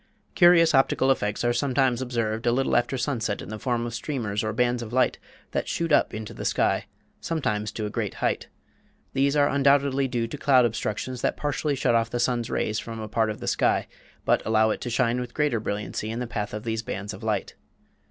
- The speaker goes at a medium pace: No, fast, 220 wpm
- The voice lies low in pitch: Yes, low, 120 Hz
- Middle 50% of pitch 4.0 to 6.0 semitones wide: No, average, 3.4 semitones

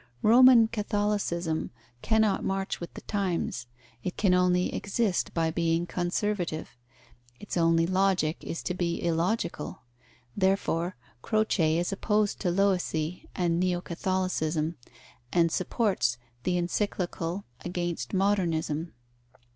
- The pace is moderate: No, slow, 110 wpm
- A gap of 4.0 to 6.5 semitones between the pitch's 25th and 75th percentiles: No, average, 3.0 semitones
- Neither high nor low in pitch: Yes, medium, 180 Hz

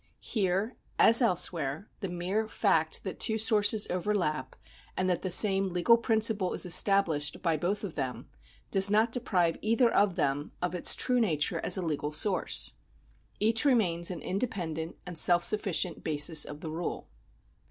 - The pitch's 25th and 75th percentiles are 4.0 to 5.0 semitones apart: Yes, average, 4.3 semitones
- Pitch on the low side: No, medium, 185 Hz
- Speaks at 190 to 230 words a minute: No, average, 165 wpm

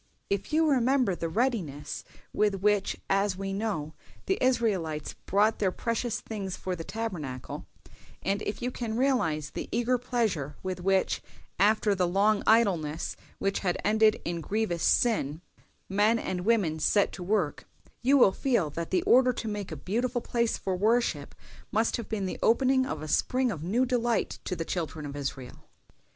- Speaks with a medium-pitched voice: No, high, 205 Hz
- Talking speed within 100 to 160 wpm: No, average, 170 wpm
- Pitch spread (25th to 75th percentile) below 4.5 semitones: No, average, 5.0 semitones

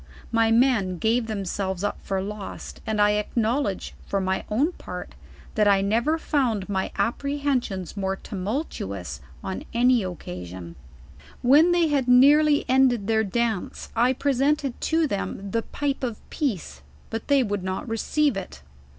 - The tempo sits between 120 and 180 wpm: Yes, average, 155 wpm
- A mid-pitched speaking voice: No, high, 225 Hz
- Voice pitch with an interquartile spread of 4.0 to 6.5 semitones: Yes, wide, 5.6 semitones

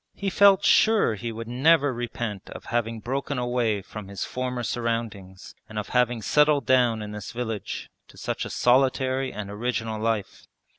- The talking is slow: No, average, 165 wpm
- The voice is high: No, low, 120 Hz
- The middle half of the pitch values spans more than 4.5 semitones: No, average, 3.1 semitones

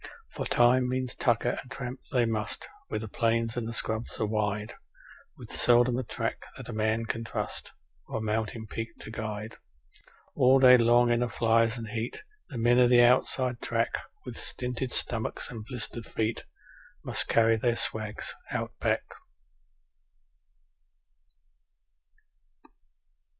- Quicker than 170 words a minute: No, average, 145 wpm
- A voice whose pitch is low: Yes, low, 115 Hz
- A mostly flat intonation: Yes, narrow, 1.8 semitones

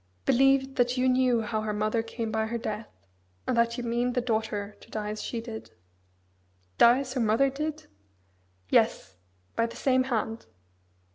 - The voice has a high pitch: Yes, high, 235 Hz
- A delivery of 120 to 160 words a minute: No, average, 170 wpm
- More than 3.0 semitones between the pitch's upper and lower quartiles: No, narrow, 2.6 semitones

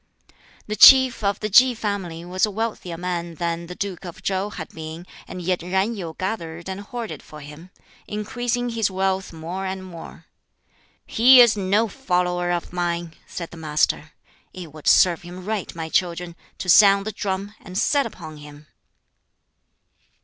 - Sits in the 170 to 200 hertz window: Yes, medium, 185 Hz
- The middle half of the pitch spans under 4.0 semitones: Yes, average, 3.4 semitones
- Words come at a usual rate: Yes, average, 165 wpm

